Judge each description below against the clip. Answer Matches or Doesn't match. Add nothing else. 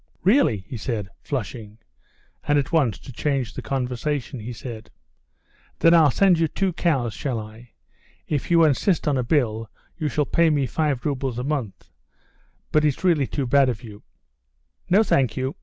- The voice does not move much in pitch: Doesn't match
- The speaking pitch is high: Doesn't match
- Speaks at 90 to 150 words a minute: Doesn't match